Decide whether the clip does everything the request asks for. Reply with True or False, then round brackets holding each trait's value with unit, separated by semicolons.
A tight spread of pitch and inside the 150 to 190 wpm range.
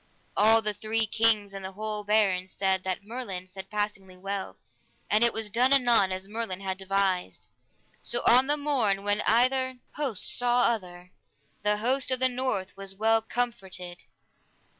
False (3.7 semitones; 160 wpm)